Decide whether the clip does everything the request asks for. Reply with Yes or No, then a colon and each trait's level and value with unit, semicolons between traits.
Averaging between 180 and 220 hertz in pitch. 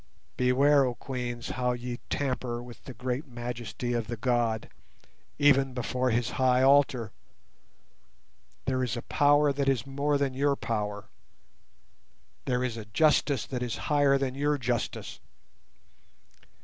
No: low, 125 Hz